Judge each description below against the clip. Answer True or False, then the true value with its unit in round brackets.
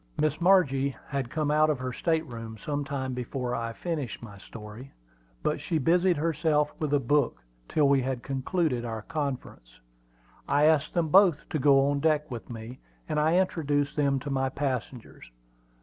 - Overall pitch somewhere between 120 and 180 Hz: True (140 Hz)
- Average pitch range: True (3.4 semitones)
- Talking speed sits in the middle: True (175 wpm)